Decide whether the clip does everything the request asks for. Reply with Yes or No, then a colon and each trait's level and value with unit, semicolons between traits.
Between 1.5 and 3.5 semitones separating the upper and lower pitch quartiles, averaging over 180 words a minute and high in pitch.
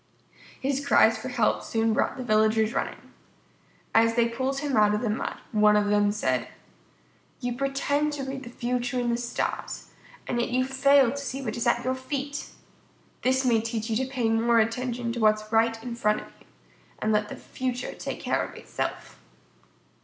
Yes: average, 2.7 semitones; average, 195 wpm; high, 240 Hz